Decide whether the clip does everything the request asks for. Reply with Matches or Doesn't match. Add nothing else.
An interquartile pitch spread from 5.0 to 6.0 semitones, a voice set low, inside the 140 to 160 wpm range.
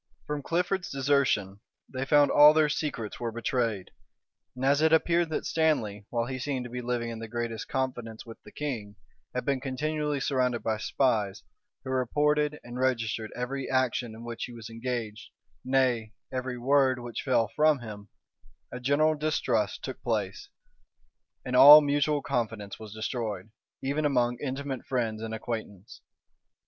Doesn't match